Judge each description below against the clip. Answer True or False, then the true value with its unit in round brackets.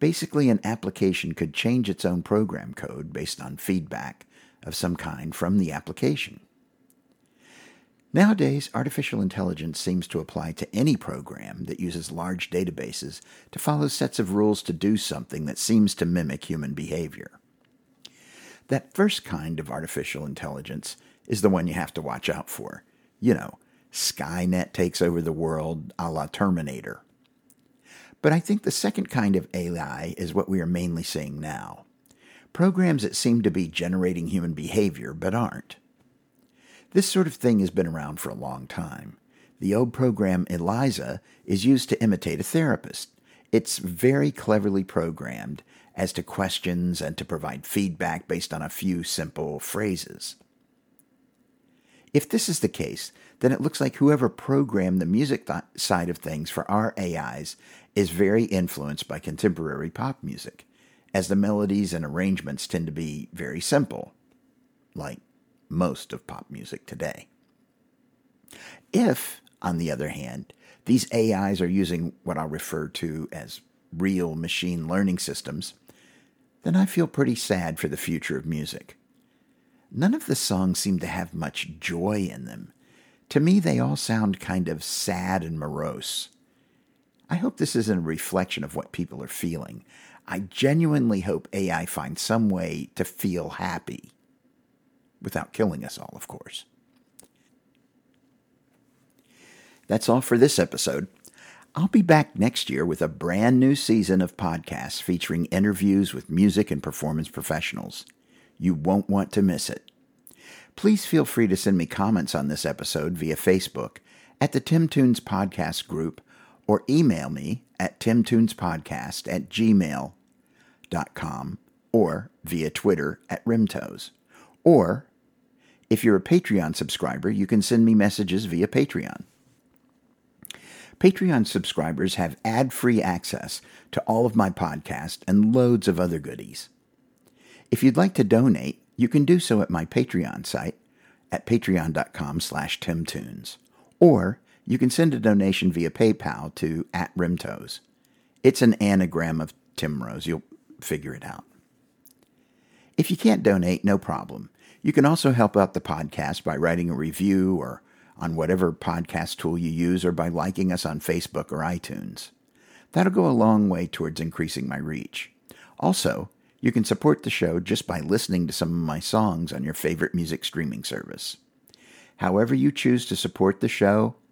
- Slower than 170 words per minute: True (155 wpm)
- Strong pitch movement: True (7.2 semitones)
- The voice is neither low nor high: False (100 Hz)